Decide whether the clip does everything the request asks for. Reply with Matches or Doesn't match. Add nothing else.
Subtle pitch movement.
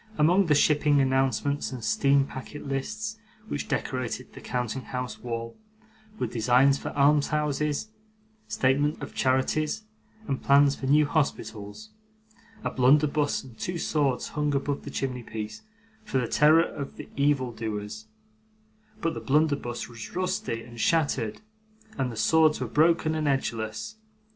Doesn't match